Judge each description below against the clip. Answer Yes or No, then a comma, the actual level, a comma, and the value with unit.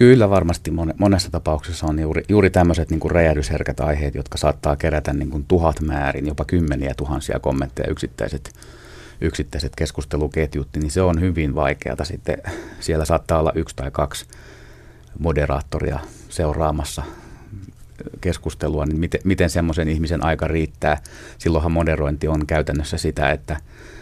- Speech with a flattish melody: Yes, narrow, 2.2 semitones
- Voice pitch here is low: Yes, very low, 80 Hz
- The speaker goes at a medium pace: Yes, average, 130 wpm